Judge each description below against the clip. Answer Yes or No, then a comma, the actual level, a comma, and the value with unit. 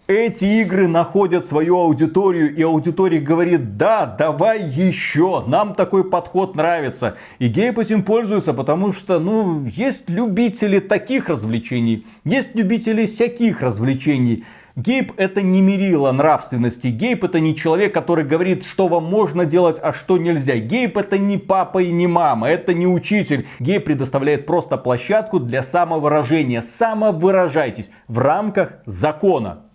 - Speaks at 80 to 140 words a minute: Yes, average, 135 wpm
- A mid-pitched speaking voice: Yes, medium, 175 Hz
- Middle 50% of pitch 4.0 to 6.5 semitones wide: Yes, average, 4.9 semitones